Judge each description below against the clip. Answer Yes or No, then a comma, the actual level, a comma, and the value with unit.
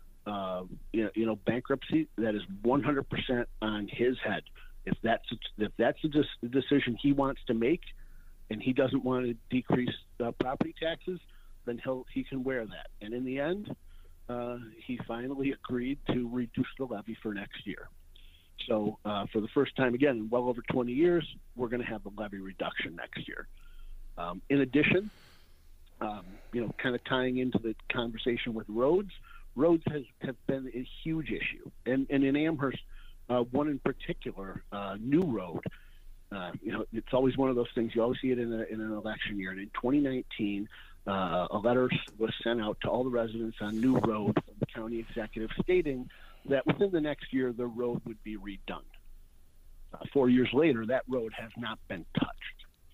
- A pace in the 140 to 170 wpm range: No, average, 190 wpm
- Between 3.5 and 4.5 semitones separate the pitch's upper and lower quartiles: Yes, average, 4.0 semitones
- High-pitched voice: No, low, 120 Hz